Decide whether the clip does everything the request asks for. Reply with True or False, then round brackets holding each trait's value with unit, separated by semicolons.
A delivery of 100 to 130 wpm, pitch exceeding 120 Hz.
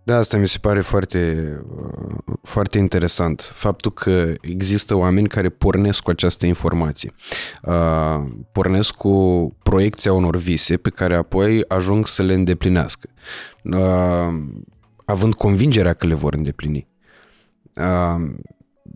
False (120 wpm; 90 Hz)